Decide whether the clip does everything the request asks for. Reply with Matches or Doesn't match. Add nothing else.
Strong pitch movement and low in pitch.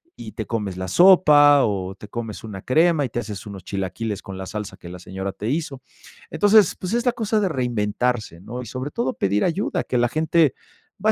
Matches